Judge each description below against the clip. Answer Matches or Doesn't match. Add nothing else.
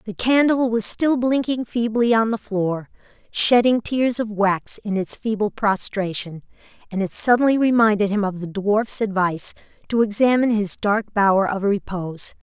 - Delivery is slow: Doesn't match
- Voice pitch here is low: Doesn't match